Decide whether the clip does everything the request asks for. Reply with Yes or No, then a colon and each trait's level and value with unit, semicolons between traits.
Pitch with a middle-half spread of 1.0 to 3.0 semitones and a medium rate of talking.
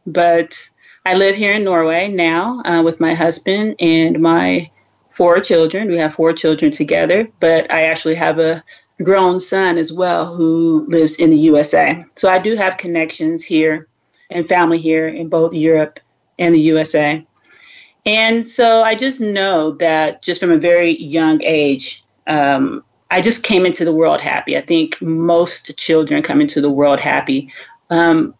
Yes: narrow, 2.4 semitones; average, 165 wpm